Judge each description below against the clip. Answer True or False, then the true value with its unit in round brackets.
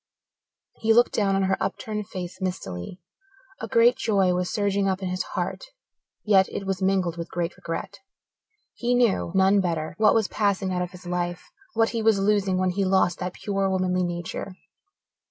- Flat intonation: True (2.1 semitones)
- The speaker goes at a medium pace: True (180 wpm)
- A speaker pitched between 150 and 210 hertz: True (190 Hz)